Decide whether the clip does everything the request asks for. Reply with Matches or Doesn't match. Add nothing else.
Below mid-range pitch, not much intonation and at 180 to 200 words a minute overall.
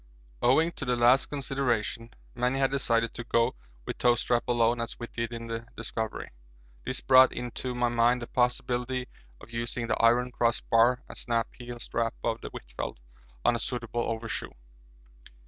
Doesn't match